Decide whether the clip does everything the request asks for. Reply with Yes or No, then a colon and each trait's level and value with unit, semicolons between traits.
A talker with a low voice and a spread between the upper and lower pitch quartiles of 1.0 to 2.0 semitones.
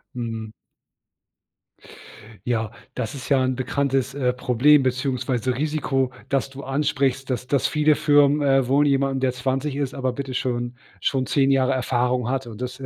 Yes: low, 130 Hz; narrow, 1.7 semitones